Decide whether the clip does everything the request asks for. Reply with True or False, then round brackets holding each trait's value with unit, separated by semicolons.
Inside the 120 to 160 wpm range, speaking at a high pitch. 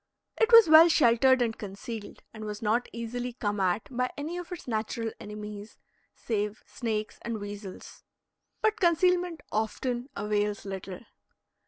True (140 wpm; 225 Hz)